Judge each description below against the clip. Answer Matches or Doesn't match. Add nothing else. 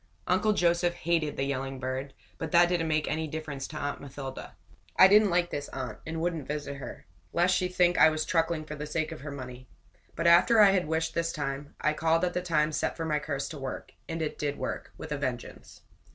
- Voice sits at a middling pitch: Matches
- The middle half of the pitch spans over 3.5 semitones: Doesn't match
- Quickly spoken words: Matches